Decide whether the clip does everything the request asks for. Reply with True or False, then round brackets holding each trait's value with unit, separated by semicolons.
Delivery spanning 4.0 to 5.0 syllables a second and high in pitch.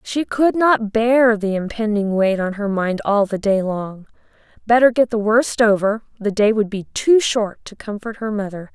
True (4.5 syllables/s; 215 Hz)